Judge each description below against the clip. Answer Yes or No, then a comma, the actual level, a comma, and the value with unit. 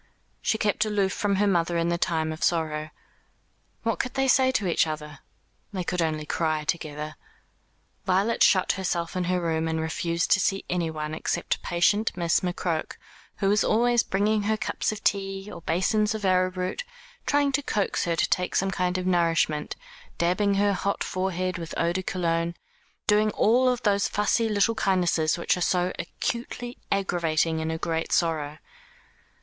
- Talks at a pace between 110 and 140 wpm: No, average, 170 wpm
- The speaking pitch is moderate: Yes, medium, 180 Hz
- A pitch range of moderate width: Yes, average, 3.7 semitones